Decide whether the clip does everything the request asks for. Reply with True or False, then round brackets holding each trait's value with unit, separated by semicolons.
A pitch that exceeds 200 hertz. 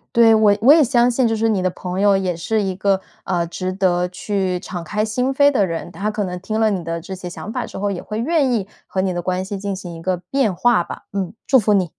False (195 Hz)